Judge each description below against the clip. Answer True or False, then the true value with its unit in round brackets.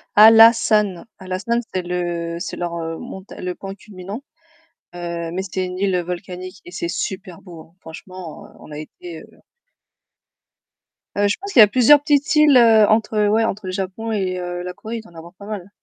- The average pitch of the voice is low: False (190 Hz)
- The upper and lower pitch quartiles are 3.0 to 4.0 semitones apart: True (3.5 semitones)